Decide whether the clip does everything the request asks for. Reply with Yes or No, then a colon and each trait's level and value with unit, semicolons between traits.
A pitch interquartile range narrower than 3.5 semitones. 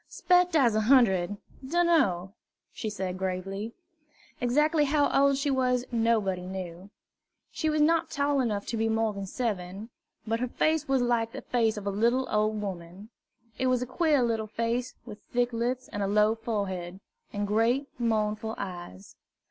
No: average, 4.3 semitones